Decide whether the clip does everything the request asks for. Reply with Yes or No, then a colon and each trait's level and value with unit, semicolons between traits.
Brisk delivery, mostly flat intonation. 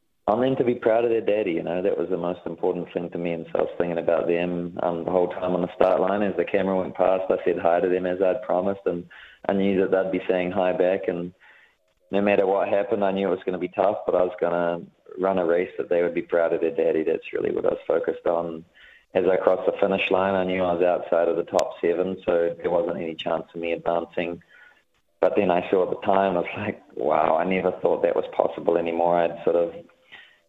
Yes: fast, 265 wpm; narrow, 2.2 semitones